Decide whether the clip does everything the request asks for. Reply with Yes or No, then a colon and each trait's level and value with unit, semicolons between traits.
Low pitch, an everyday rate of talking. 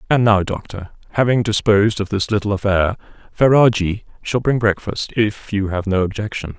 Yes: low, 105 Hz; average, 165 wpm